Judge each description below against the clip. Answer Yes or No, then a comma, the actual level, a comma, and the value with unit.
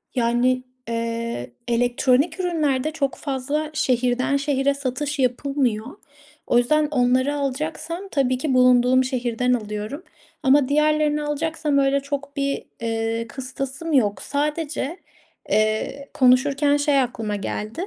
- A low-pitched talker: No, very high, 270 Hz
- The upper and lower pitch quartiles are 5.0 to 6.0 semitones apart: No, average, 3.0 semitones